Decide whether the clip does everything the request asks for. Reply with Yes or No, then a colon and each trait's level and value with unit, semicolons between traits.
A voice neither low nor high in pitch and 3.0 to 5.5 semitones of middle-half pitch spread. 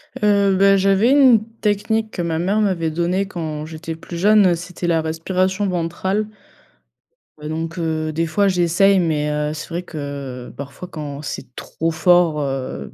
Yes: medium, 170 Hz; average, 3.7 semitones